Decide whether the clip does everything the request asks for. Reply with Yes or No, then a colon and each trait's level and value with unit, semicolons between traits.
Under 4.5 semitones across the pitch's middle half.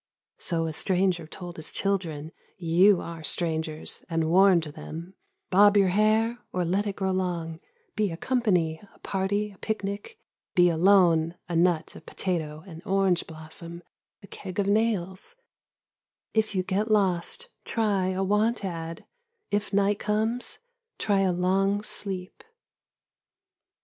Yes: average, 3.3 semitones